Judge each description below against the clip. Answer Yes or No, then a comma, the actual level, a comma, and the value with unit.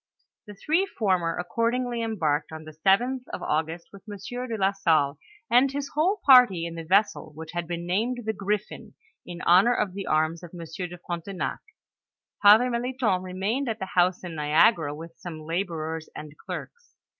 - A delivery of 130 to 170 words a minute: No, average, 180 wpm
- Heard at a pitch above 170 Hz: Yes, medium, 185 Hz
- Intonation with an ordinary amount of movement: No, wide, 5.7 semitones